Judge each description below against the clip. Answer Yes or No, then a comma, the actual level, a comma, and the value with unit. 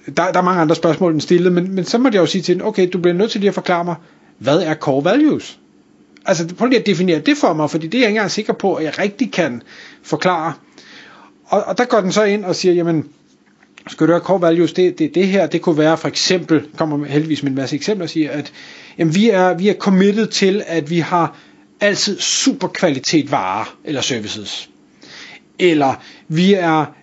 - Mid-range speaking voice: Yes, medium, 180 Hz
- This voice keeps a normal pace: No, fast, 230 wpm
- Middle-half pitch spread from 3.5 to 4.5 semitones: Yes, average, 3.8 semitones